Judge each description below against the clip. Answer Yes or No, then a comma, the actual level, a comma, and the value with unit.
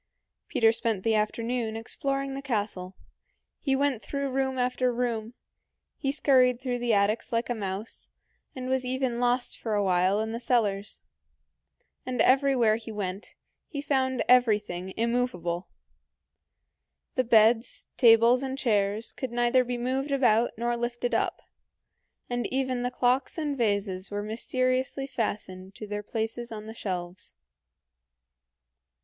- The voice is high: Yes, high, 235 Hz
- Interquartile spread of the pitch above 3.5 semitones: No, average, 3.2 semitones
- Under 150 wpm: Yes, average, 140 wpm